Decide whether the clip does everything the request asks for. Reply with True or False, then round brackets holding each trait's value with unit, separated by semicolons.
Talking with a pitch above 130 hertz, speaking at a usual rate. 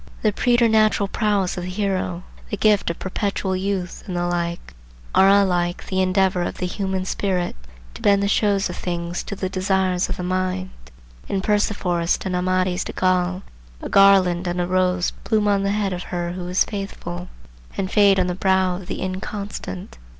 True (185 Hz; 185 wpm)